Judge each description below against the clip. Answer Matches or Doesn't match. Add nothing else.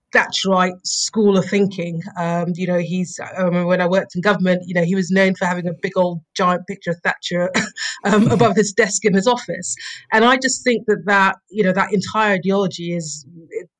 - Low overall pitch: Doesn't match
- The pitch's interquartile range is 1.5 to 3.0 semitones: Matches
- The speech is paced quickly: Matches